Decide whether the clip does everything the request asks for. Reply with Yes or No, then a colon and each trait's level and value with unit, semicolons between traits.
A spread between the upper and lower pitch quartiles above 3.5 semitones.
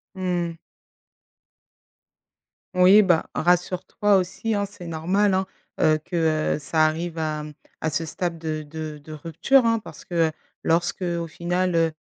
No: narrow, 2.6 semitones